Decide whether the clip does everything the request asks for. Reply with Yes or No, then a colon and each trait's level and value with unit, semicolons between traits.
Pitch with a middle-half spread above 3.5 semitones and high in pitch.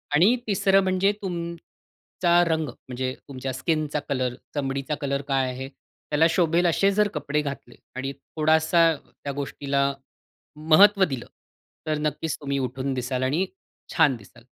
No: average, 3.9 semitones; medium, 150 Hz